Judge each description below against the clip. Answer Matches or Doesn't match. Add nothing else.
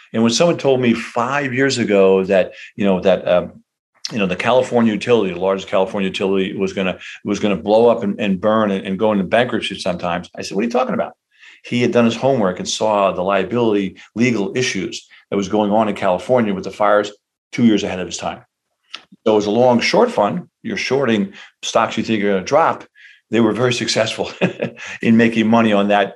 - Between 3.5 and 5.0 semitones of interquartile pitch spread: Doesn't match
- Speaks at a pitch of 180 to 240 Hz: Doesn't match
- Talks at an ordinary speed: Doesn't match